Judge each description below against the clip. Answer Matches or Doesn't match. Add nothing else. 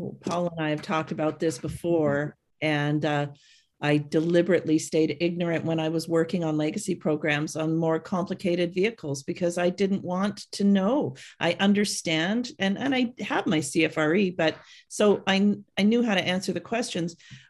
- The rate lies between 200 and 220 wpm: Doesn't match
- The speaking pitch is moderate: Matches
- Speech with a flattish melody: Doesn't match